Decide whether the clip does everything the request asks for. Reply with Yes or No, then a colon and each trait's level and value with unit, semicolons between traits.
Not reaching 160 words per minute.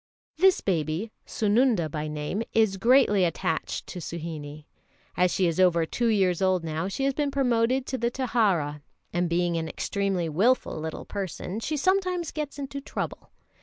No: average, 165 wpm